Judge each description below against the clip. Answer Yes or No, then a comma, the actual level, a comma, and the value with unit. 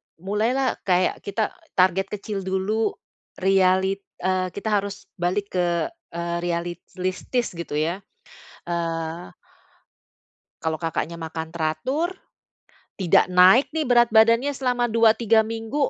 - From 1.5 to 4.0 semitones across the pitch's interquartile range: No, average, 4.5 semitones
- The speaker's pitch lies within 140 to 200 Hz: Yes, high, 190 Hz